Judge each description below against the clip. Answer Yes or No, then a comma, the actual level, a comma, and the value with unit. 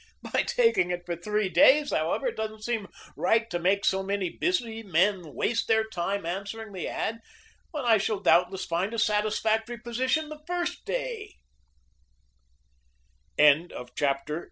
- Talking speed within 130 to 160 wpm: Yes, average, 150 wpm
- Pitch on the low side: No, high, 215 Hz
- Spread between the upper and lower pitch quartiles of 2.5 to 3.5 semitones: No, average, 4.9 semitones